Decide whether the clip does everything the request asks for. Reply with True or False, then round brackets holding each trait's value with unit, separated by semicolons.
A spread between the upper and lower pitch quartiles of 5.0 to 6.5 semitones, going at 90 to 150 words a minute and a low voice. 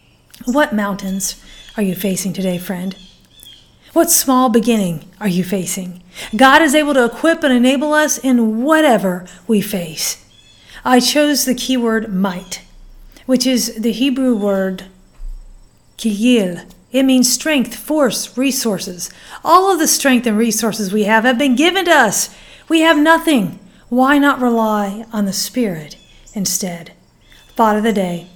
False (5.6 semitones; 145 wpm; 225 Hz)